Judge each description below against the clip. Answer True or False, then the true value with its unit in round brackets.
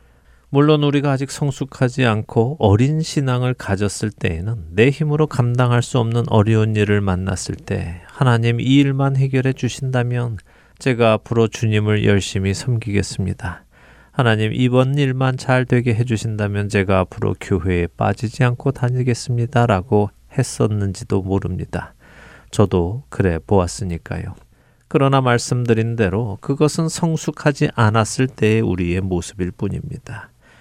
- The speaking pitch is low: True (115 Hz)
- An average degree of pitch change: True (4.5 semitones)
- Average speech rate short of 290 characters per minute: False (310 characters per minute)